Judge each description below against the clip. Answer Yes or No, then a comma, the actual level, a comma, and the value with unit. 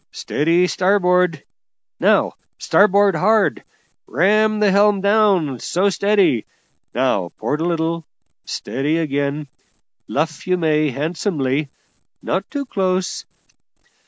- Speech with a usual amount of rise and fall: Yes, average, 4.9 semitones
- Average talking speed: No, slow, 100 wpm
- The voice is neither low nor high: Yes, medium, 175 Hz